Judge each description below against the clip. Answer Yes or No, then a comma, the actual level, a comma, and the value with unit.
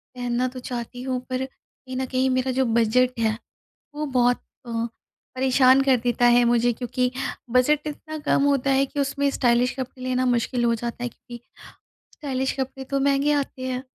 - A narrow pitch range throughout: Yes, narrow, 1.6 semitones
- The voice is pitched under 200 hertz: No, very high, 255 Hz